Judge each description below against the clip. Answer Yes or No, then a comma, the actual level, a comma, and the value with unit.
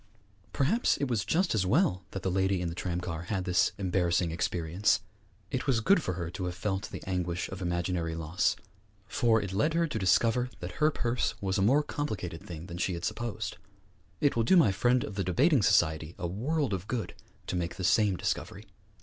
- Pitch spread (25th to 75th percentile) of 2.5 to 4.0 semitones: No, average, 5.0 semitones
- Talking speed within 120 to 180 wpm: No, fast, 205 wpm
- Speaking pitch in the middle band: No, very low, 95 Hz